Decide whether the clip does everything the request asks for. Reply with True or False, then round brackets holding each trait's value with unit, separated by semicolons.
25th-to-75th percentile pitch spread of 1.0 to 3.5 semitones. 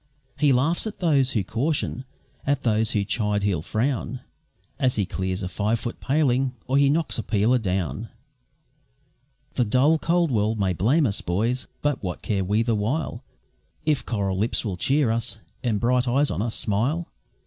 False (5.0 semitones)